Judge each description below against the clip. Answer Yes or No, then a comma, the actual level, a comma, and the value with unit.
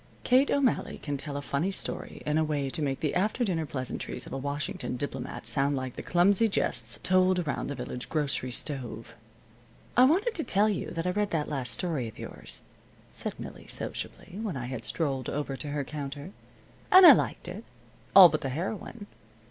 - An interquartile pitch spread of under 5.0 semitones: No, wide, 5.5 semitones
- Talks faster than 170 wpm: Yes, average, 195 wpm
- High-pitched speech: No, medium, 150 Hz